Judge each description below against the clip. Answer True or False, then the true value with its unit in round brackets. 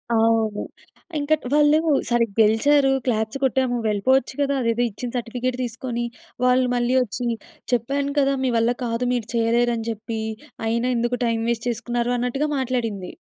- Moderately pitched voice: False (240 Hz)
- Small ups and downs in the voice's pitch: True (2.2 semitones)